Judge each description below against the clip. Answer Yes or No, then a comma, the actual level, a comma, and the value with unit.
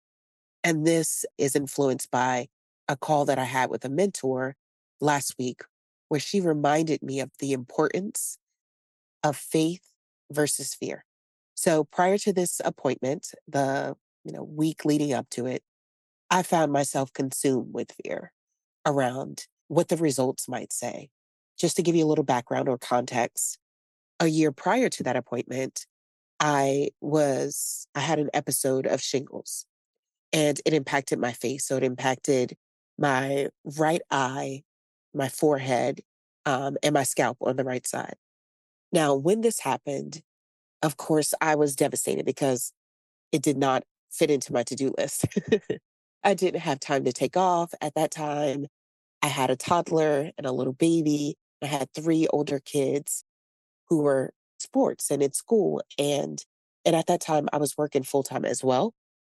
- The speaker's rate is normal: Yes, average, 155 wpm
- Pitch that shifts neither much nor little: Yes, average, 3.3 semitones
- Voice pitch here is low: No, medium, 145 Hz